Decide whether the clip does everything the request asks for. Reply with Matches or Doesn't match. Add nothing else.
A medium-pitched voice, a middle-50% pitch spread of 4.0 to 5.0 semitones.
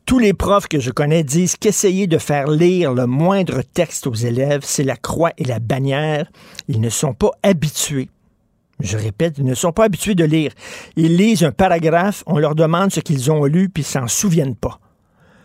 Matches